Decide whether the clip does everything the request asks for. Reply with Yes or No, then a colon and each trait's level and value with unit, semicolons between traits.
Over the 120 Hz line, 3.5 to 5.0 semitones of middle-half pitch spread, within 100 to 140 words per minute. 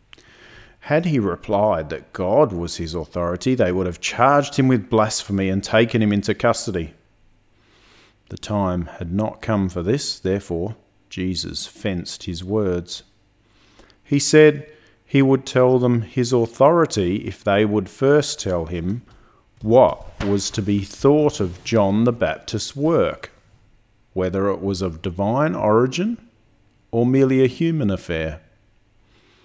No: low, 110 Hz; average, 4.1 semitones; slow, 135 wpm